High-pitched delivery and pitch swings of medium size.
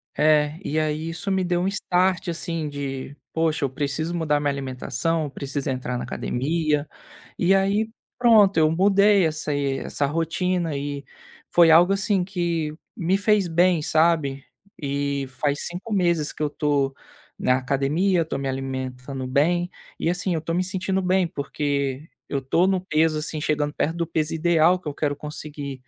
No: medium, 155 Hz; average, 3.8 semitones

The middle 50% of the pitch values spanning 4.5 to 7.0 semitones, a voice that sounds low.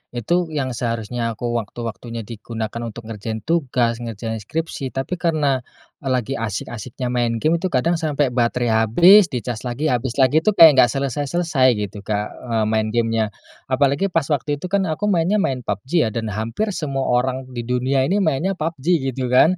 Yes: average, 5.0 semitones; low, 125 Hz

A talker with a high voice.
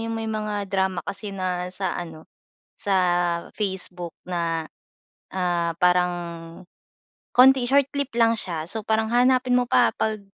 Yes: high, 200 Hz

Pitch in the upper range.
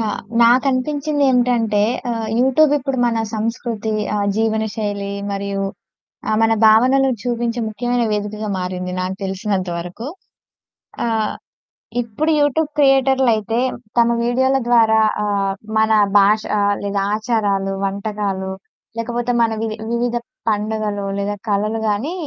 Yes: high, 220 Hz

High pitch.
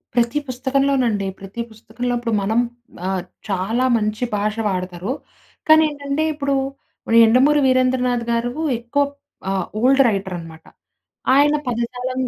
Yes: high, 240 Hz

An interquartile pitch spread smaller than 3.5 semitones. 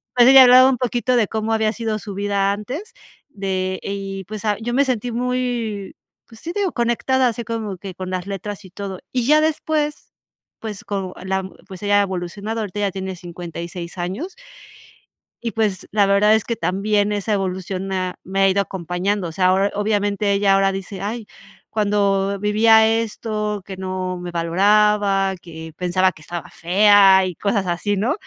Yes: average, 2.7 semitones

